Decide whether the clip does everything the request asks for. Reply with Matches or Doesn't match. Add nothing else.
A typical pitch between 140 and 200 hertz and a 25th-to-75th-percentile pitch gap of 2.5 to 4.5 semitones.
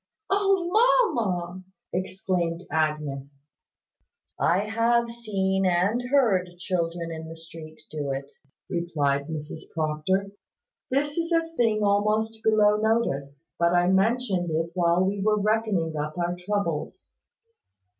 Doesn't match